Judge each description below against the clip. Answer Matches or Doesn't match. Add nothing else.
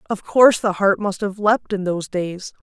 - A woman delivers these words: Matches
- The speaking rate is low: Doesn't match